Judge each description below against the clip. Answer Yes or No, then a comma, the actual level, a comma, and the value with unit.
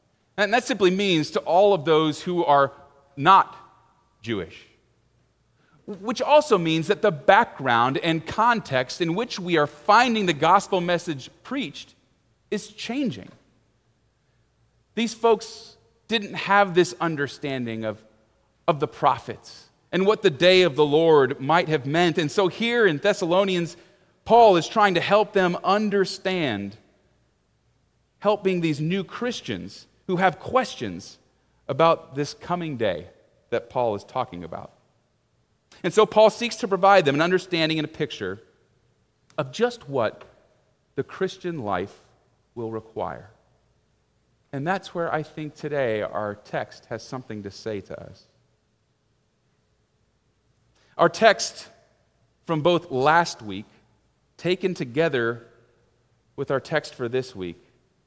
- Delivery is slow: Yes, slow, 130 wpm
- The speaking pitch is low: No, medium, 170 Hz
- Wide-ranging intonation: Yes, wide, 6.4 semitones